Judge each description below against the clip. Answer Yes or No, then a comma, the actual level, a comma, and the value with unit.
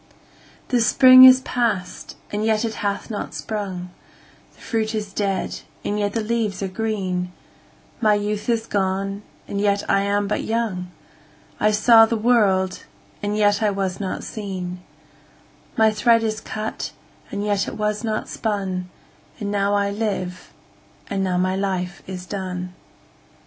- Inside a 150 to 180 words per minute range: No, average, 140 wpm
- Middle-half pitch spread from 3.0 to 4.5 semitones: No, narrow, 2.4 semitones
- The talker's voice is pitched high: Yes, high, 205 Hz